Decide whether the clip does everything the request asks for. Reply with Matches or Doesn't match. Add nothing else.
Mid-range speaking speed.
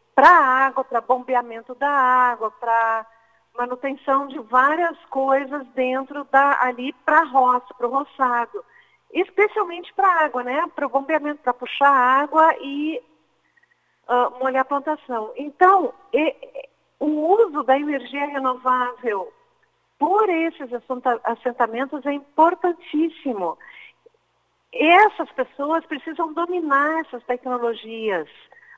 Doesn't match